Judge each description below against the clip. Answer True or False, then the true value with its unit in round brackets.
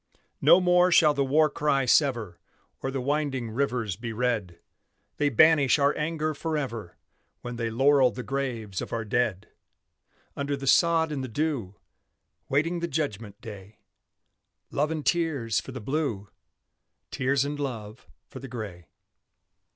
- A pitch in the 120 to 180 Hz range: True (135 Hz)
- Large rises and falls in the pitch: False (4.8 semitones)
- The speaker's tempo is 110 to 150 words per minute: True (145 wpm)